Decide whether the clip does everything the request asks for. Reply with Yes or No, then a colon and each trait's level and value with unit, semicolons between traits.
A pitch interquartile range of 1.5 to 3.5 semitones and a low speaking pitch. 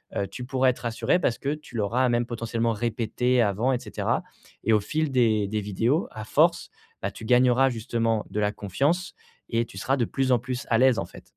Yes: average, 2.9 semitones; low, 120 Hz